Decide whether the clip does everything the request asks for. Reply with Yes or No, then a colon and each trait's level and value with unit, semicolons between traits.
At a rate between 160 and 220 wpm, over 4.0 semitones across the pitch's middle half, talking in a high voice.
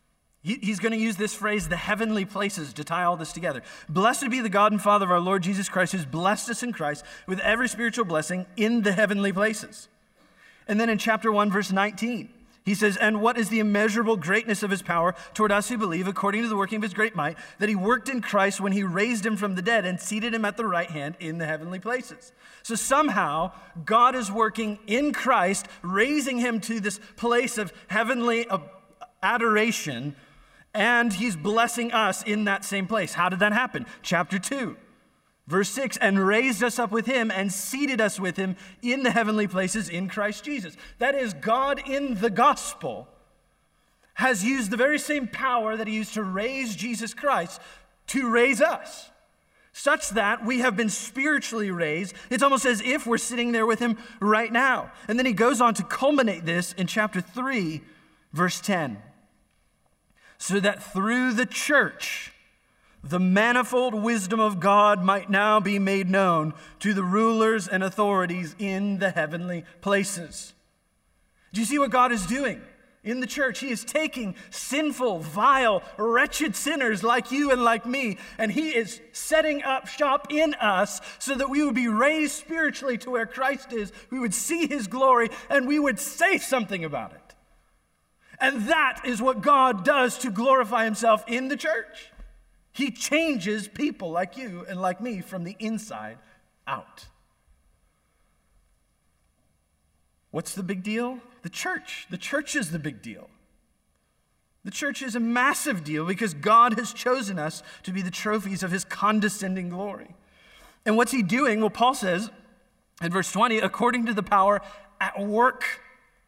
Yes: average, 175 wpm; average, 4.4 semitones; high, 220 Hz